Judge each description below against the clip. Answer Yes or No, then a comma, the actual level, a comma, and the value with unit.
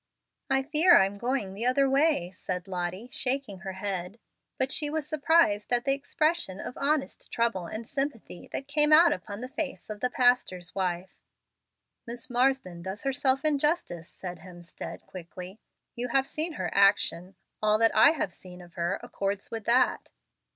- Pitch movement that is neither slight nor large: No, wide, 6.6 semitones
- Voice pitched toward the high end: Yes, high, 230 Hz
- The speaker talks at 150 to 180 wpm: Yes, average, 165 wpm